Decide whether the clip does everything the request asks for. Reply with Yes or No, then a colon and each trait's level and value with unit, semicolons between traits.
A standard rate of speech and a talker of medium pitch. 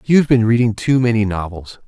No: average, 190 wpm; low, 115 Hz